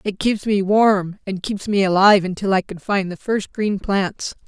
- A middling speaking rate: No, fast, 215 wpm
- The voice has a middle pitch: No, high, 195 Hz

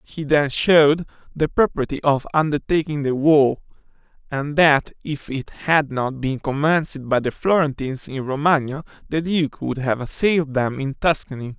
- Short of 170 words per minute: Yes, average, 155 wpm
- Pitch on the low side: No, medium, 145 Hz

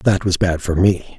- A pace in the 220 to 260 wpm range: Yes, fast, 255 wpm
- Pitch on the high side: No, very low, 90 Hz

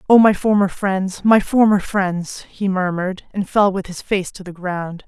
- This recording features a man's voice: No, female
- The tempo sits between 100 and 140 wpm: No, average, 200 wpm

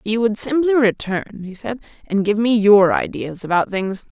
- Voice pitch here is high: Yes, high, 215 Hz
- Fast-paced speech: No, average, 185 wpm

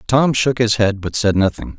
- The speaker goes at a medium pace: No, fast, 235 wpm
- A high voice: No, low, 110 Hz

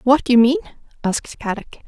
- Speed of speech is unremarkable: Yes, average, 160 wpm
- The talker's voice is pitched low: No, high, 235 Hz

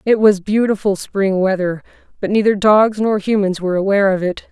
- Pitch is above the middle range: Yes, high, 200 Hz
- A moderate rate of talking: Yes, average, 185 wpm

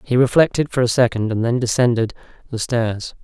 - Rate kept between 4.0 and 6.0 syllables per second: Yes, 5.5 syllables/s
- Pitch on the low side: Yes, low, 120 Hz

